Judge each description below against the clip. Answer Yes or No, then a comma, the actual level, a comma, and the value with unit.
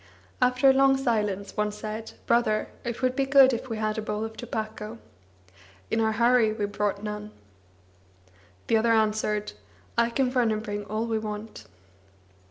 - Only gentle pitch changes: Yes, narrow, 2.1 semitones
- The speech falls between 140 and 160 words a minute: No, average, 170 wpm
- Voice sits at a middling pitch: No, high, 220 Hz